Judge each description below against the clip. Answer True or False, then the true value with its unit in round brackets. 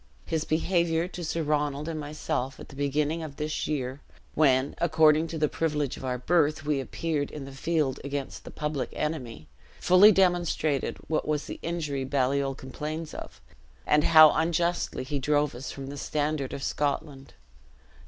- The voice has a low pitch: False (150 Hz)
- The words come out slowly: False (165 wpm)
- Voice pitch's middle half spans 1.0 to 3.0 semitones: True (2.5 semitones)